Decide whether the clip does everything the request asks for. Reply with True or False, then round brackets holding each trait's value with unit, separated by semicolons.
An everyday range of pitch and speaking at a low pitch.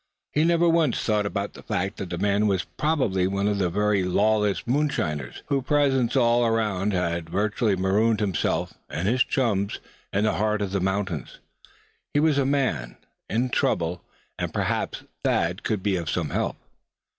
True (4.3 semitones; 105 Hz)